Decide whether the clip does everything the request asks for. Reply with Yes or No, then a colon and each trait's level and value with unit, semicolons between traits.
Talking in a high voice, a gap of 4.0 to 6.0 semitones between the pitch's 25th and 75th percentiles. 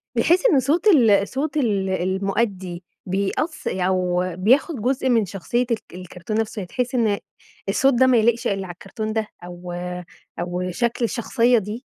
Yes: high, 215 Hz; average, 4.8 semitones